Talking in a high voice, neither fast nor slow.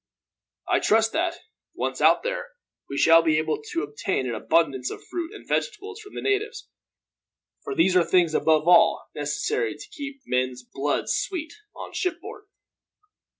No: medium, 180 Hz; average, 155 wpm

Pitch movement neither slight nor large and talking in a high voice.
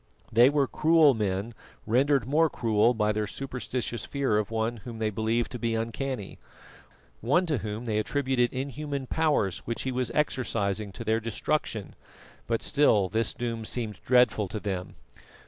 No: average, 3.8 semitones; low, 115 Hz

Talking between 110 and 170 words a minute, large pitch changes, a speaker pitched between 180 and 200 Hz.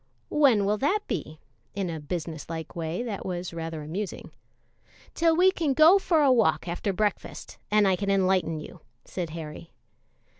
Yes: average, 165 wpm; wide, 7.0 semitones; high, 190 Hz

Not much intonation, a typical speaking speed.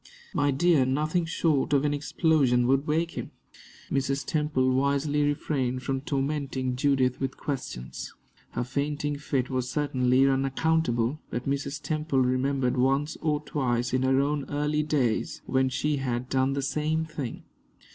Yes: narrow, 2.3 semitones; average, 145 wpm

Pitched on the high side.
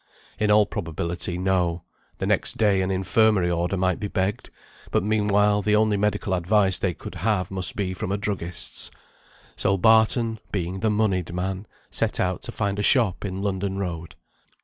No: very low, 95 Hz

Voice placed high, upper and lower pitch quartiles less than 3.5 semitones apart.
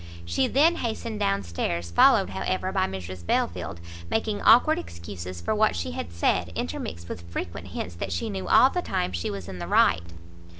No: very low, 90 Hz; average, 2.7 semitones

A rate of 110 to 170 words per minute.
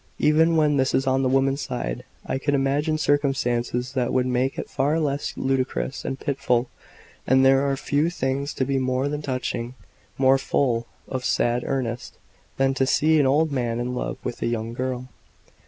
No: average, 180 wpm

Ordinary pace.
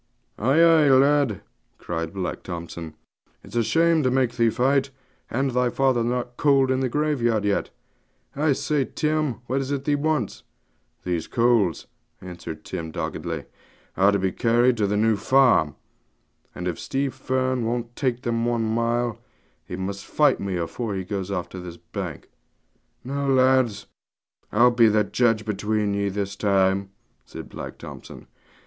Yes: average, 155 wpm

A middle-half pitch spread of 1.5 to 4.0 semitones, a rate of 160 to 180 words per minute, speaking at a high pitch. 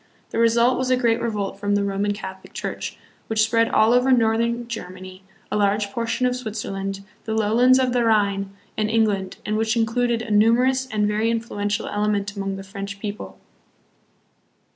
Yes: narrow, 2.5 semitones; average, 170 wpm; high, 220 Hz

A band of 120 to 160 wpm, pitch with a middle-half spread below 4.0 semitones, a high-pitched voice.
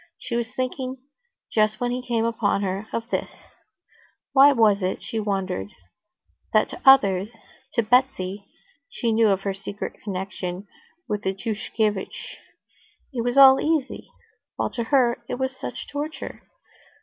No: average, 140 wpm; average, 4.3 semitones; high, 225 Hz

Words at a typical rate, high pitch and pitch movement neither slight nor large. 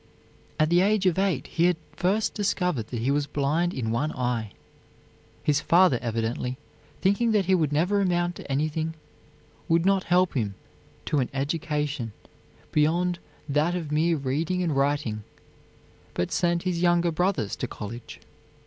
No: average, 155 wpm; medium, 155 Hz; average, 4.6 semitones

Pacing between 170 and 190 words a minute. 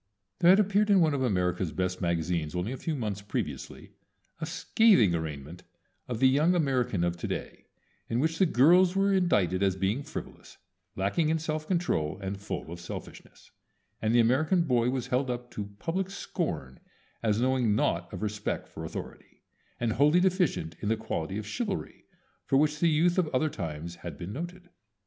Yes: average, 180 wpm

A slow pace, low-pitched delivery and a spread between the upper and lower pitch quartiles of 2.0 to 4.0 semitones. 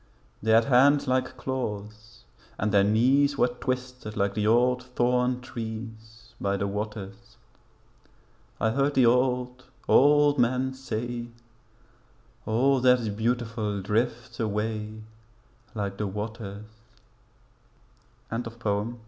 Yes: slow, 115 wpm; low, 115 Hz; average, 2.8 semitones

